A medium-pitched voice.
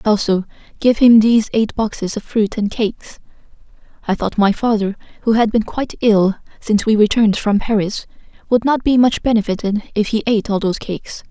No: high, 215 Hz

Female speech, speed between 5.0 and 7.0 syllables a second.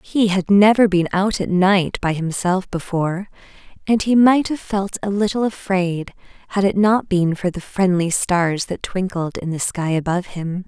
No: female; 4.5 syllables/s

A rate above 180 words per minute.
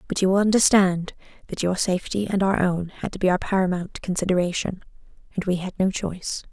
Yes: average, 195 wpm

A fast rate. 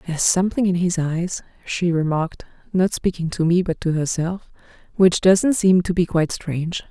No: average, 185 wpm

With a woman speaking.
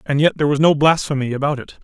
No: male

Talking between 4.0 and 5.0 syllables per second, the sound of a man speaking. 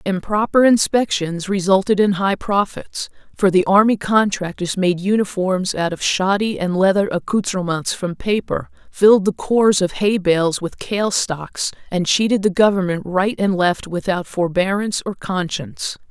No: 4.5 syllables/s; female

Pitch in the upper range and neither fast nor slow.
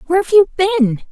Yes: very high, 340 Hz; average, 160 wpm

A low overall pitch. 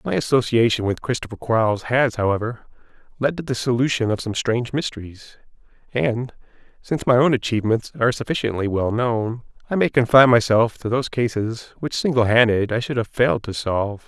Yes: low, 120 Hz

